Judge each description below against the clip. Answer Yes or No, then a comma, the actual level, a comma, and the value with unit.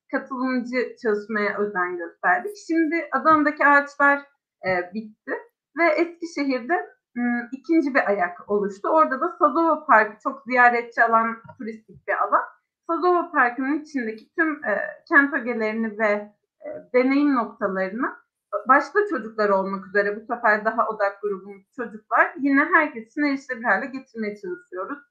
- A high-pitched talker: Yes, very high, 260 Hz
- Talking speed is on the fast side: No, average, 115 wpm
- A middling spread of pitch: No, wide, 6.1 semitones